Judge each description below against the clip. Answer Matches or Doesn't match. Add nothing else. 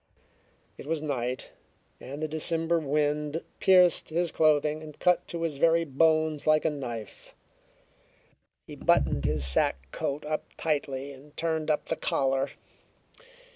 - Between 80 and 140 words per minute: Matches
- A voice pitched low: Doesn't match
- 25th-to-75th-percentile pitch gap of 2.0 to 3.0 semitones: Matches